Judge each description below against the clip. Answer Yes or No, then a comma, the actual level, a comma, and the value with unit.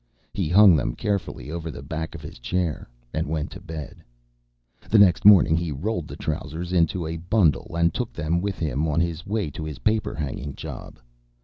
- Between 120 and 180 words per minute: No, average, 195 wpm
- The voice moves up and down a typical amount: Yes, average, 3.4 semitones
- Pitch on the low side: Yes, very low, 85 Hz